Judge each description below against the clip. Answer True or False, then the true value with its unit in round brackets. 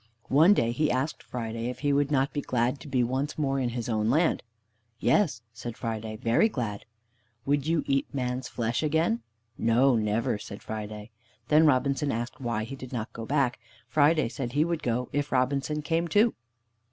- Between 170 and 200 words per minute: True (185 wpm)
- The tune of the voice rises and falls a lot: False (3.8 semitones)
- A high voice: False (130 Hz)